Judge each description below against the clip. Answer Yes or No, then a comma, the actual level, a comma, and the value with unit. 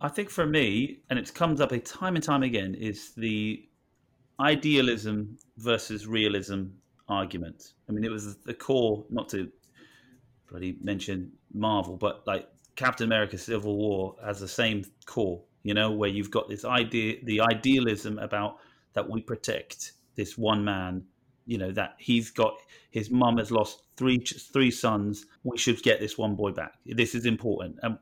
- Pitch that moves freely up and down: No, average, 3.3 semitones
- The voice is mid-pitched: No, low, 110 Hz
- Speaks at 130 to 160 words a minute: No, average, 170 wpm